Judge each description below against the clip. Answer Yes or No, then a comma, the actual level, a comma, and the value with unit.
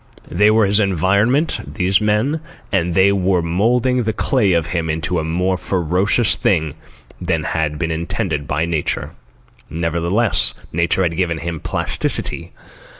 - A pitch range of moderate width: Yes, average, 3.9 semitones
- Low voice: Yes, very low, 90 Hz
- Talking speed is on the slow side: No, average, 145 wpm